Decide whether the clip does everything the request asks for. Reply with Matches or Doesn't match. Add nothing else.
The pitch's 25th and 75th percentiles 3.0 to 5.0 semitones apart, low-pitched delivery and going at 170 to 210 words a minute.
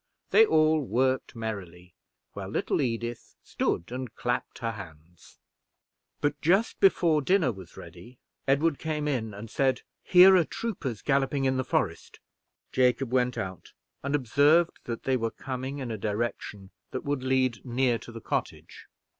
Doesn't match